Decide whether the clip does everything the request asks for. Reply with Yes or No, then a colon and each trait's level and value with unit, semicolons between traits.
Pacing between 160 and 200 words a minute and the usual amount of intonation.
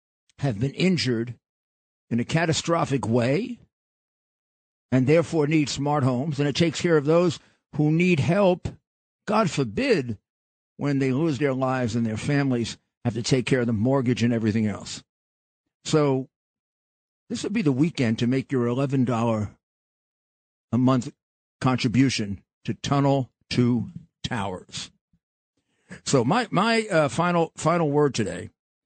No: slow, 135 wpm; average, 4.8 semitones